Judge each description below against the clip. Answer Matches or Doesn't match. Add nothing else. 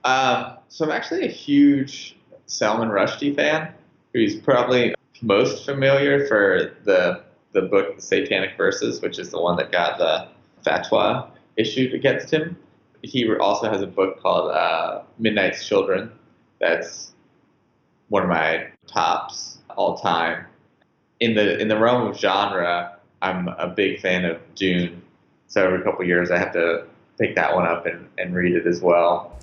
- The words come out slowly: Doesn't match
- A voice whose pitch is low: Matches